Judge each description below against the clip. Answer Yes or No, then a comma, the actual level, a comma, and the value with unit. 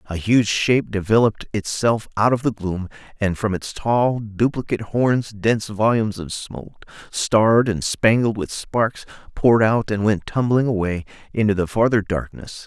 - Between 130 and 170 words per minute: Yes, average, 160 wpm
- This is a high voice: No, low, 110 Hz